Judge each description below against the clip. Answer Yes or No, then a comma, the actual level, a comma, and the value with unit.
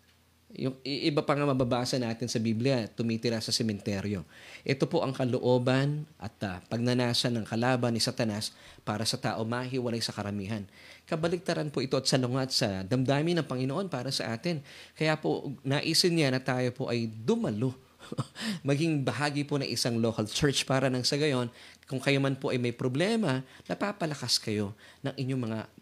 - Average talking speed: No, fast, 170 wpm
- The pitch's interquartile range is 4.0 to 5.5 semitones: No, average, 3.4 semitones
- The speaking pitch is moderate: No, low, 130 Hz